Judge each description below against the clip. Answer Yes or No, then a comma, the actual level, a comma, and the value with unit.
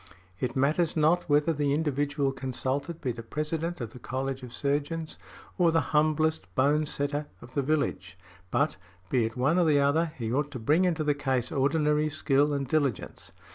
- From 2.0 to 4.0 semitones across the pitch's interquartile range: Yes, average, 2.8 semitones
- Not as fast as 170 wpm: No, average, 180 wpm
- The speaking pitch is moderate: Yes, medium, 145 Hz